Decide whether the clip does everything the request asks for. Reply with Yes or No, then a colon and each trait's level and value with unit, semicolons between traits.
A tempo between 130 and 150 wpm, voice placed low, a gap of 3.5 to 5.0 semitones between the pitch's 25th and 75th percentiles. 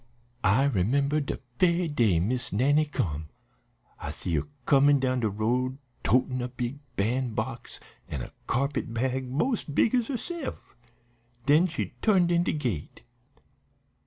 Yes: average, 145 wpm; low, 130 Hz; average, 4.7 semitones